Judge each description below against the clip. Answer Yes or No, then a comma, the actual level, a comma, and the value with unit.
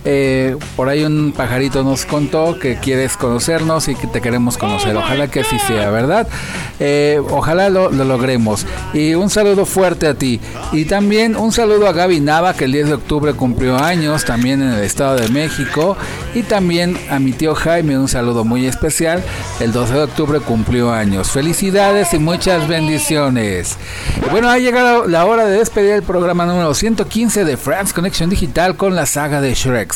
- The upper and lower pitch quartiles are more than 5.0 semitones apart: Yes, wide, 5.5 semitones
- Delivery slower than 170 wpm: No, average, 180 wpm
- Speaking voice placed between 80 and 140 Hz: No, medium, 150 Hz